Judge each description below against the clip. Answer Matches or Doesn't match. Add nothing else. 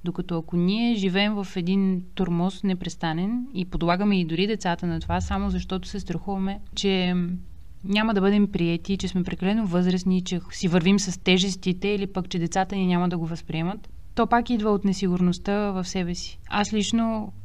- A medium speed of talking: Doesn't match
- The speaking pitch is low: Doesn't match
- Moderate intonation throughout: Doesn't match